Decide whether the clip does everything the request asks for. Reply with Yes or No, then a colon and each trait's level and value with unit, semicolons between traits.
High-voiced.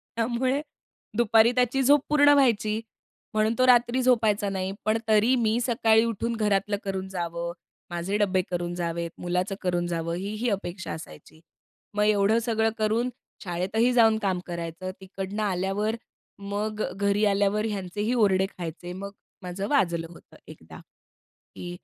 Yes: high, 205 Hz